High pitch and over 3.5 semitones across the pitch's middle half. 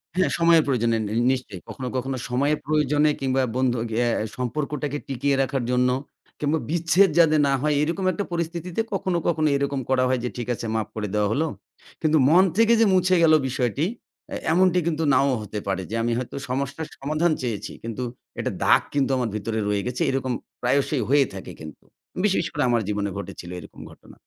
No: medium, 140 Hz; average, 4.5 semitones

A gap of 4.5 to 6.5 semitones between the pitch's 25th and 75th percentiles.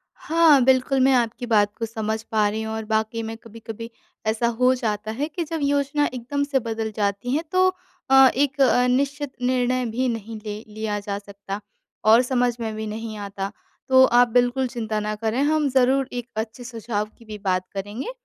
No: average, 3.2 semitones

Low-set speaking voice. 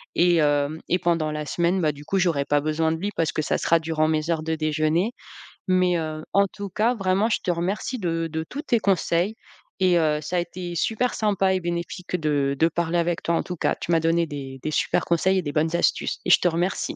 No: medium, 170 Hz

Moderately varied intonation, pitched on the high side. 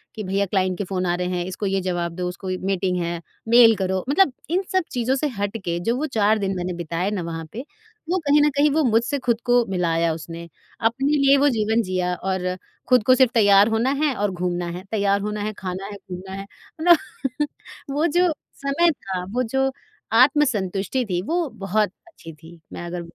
No: wide, 5.9 semitones; high, 205 Hz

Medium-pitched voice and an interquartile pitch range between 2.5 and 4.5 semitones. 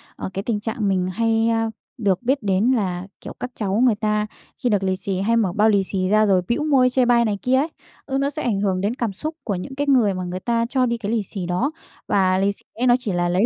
No: high, 215 Hz; average, 4.1 semitones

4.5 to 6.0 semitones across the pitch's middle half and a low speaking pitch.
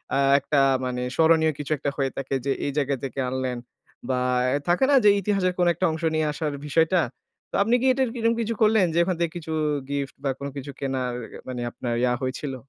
No: average, 4.8 semitones; medium, 150 Hz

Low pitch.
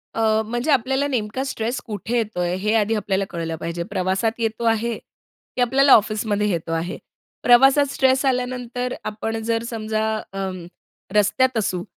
No: high, 225 Hz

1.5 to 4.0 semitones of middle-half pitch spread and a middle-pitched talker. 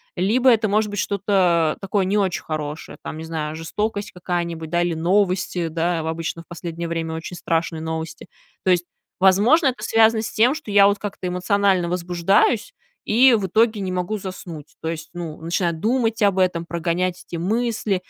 Yes: average, 3.7 semitones; medium, 180 Hz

